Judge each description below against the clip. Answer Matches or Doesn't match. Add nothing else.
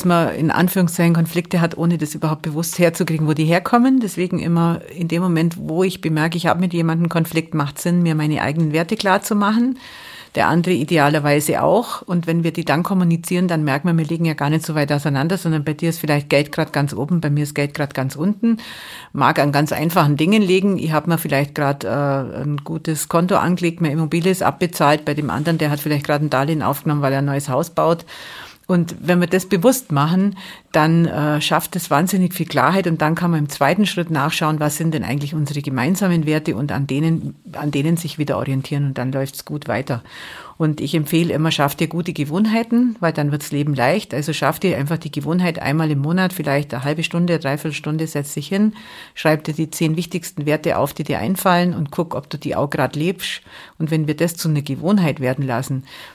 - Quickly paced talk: Matches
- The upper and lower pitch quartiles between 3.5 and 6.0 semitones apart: Doesn't match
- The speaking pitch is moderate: Matches